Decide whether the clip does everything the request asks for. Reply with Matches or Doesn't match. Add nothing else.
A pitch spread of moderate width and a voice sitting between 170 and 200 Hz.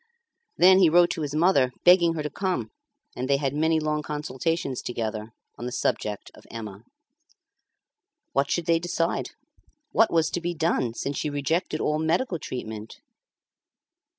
Doesn't match